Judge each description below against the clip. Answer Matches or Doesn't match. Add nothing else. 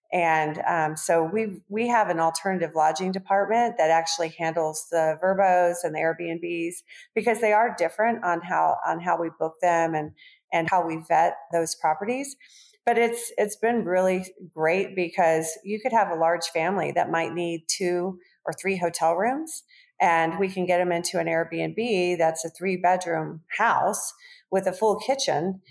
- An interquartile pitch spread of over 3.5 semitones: Matches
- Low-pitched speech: Doesn't match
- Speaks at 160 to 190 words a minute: Matches